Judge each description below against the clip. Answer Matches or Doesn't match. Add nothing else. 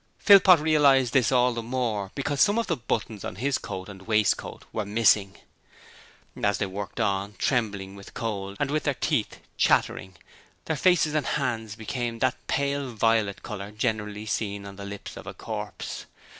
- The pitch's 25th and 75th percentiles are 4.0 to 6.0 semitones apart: Matches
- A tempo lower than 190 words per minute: Matches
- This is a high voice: Doesn't match